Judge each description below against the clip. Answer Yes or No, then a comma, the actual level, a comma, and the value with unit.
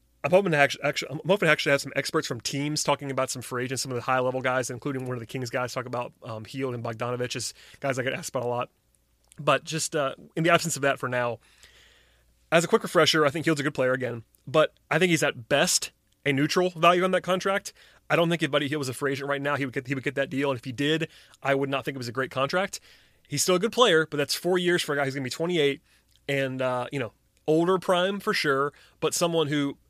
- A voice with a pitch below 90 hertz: No, medium, 140 Hz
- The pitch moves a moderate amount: Yes, average, 3.7 semitones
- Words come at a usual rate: No, fast, 275 wpm